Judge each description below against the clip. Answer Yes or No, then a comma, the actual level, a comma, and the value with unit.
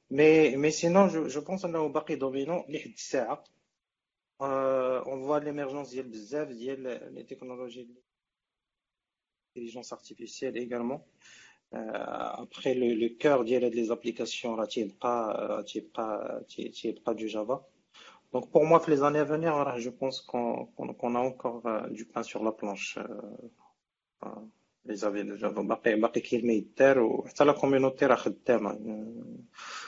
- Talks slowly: No, average, 120 wpm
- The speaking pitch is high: No, low, 125 Hz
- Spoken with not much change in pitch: No, average, 3.6 semitones